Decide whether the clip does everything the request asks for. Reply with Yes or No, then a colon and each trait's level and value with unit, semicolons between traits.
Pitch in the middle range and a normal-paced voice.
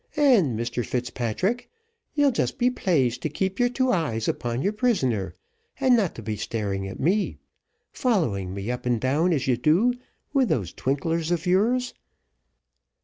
Yes: medium, 155 Hz; average, 155 wpm